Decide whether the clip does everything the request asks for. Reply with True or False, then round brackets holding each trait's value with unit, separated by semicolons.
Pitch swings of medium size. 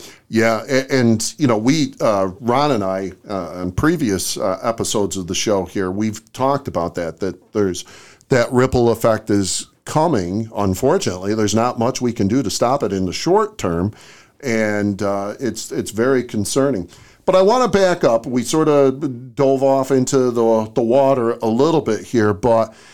True (4.4 semitones)